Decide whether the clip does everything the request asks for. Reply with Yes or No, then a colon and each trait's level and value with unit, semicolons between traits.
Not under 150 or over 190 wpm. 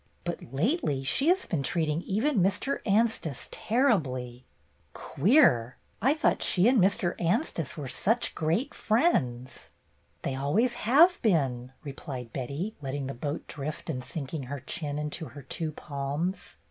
No: average, 140 wpm